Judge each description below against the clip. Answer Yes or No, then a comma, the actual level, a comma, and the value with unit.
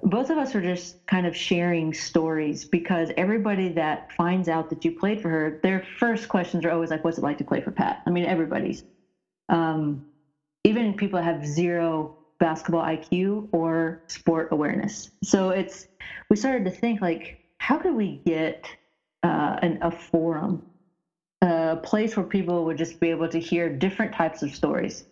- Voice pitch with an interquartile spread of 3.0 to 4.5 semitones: No, narrow, 2.6 semitones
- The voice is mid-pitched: Yes, medium, 170 Hz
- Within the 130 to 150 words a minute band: No, average, 175 wpm